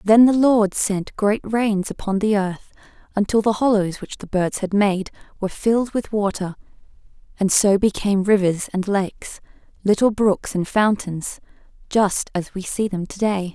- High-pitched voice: Yes, high, 200 Hz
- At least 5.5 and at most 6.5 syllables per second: No, 4.5 syllables/s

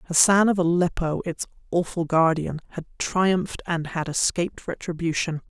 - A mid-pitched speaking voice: Yes, medium, 170 Hz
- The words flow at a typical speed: No, slow, 130 wpm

